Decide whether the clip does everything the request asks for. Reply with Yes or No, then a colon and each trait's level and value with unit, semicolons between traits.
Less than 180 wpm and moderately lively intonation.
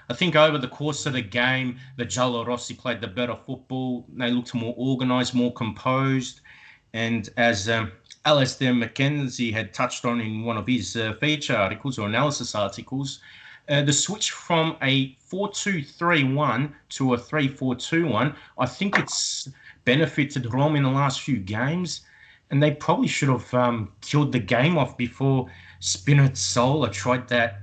Yes: average, 160 wpm; average, 3.1 semitones